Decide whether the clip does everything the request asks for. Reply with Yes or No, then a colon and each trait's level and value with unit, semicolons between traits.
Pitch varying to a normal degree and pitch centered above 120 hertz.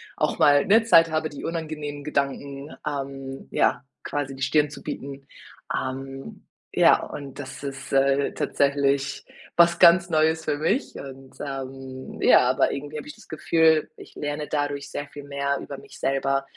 No: narrow, 1.9 semitones; medium, 140 Hz